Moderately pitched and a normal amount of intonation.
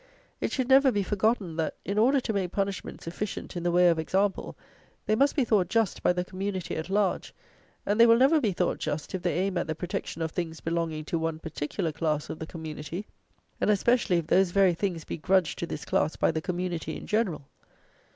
Yes: medium, 180 Hz; average, 4.0 semitones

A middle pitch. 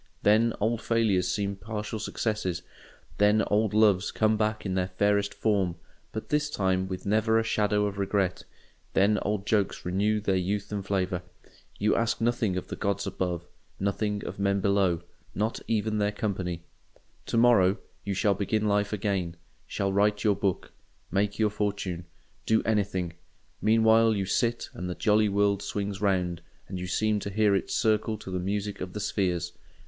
No: low, 100 Hz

